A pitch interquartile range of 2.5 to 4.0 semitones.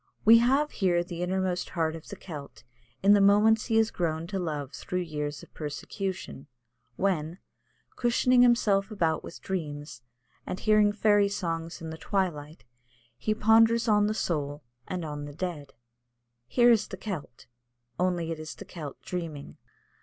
No: average, 4.8 semitones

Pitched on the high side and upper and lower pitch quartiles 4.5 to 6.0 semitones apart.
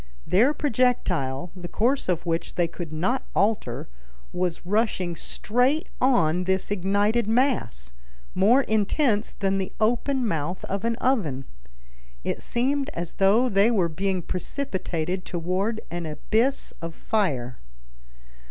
Yes: high, 195 Hz; wide, 5.4 semitones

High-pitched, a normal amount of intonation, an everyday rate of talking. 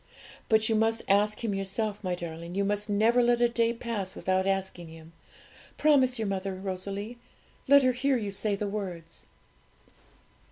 Yes: high, 205 Hz; average, 3.5 semitones; average, 165 wpm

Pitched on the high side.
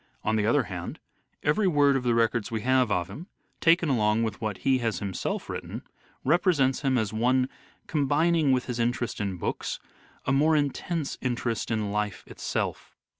No: low, 125 Hz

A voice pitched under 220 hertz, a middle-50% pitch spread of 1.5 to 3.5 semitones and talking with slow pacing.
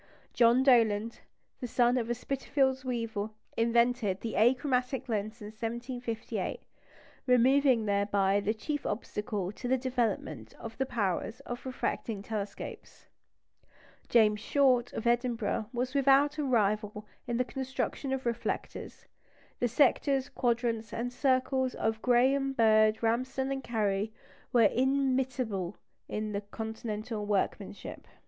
No: high, 235 Hz; average, 3.1 semitones; slow, 120 wpm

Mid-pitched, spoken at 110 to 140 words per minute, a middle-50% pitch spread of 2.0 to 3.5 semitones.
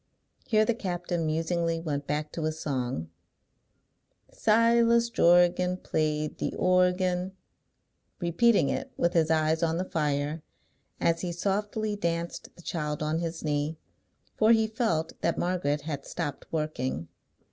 Yes: medium, 170 Hz; slow, 135 wpm; average, 3.0 semitones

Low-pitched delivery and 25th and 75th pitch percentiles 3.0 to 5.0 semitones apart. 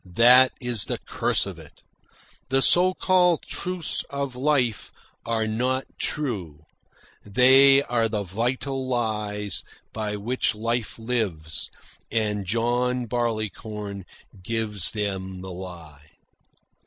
Yes: low, 115 Hz; average, 3.8 semitones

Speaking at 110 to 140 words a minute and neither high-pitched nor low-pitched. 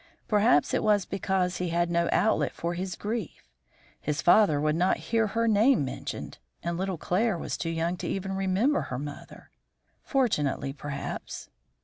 No: average, 160 wpm; medium, 180 Hz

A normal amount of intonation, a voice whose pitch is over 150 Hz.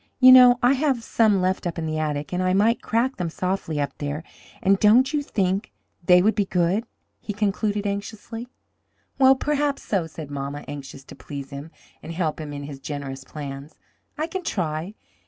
No: wide, 7.0 semitones; medium, 185 Hz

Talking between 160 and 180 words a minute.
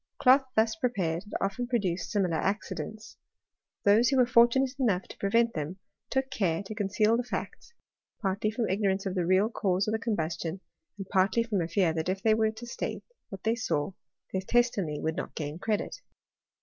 No: average, 190 wpm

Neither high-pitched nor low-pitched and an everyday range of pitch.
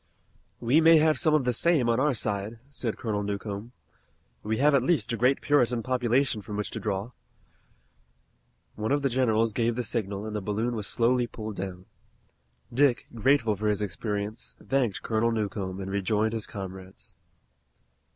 No: low, 115 Hz; average, 3.5 semitones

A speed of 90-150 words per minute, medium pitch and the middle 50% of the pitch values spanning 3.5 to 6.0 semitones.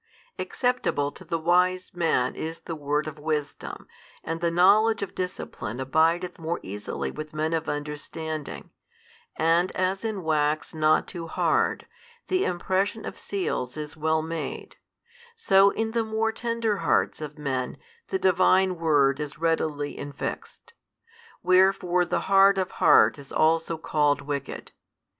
Yes: average, 140 wpm; medium, 165 Hz; average, 3.8 semitones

